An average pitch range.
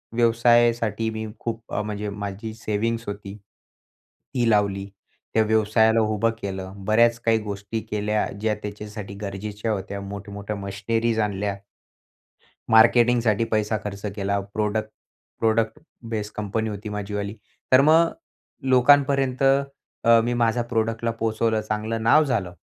No: narrow, 2.0 semitones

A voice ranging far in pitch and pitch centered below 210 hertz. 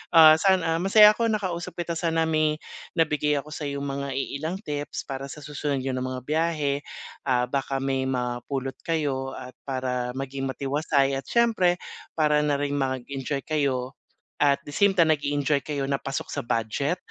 No: average, 2.9 semitones; medium, 140 Hz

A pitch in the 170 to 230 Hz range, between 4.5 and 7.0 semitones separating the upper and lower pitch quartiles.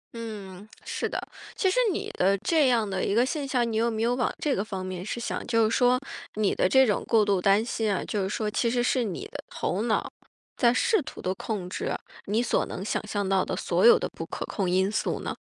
No: high, 220 Hz; average, 3.8 semitones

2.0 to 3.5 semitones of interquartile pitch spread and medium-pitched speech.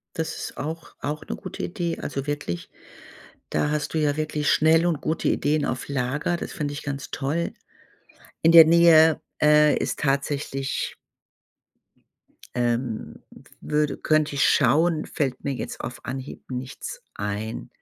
Yes: narrow, 2.6 semitones; medium, 145 Hz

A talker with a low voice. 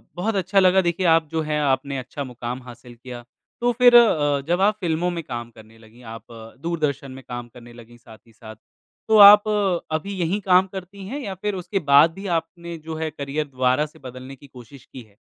No: medium, 150 Hz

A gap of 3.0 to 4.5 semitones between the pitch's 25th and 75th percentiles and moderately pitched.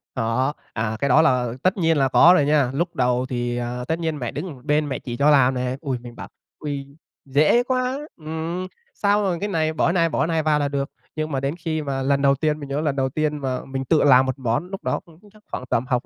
Yes: average, 3.8 semitones; medium, 145 Hz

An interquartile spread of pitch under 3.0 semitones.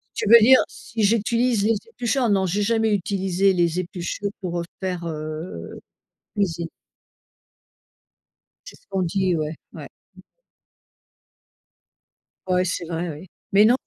No: average, 3.8 semitones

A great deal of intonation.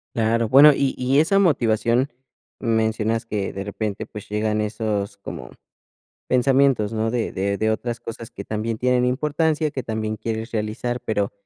No: average, 2.8 semitones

